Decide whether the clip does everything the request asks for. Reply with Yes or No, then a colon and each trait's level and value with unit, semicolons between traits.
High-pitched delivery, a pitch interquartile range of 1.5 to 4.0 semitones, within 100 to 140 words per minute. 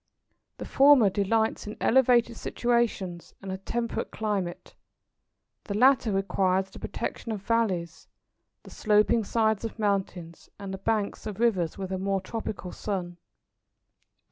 Yes: high, 205 Hz; average, 3.2 semitones; slow, 135 wpm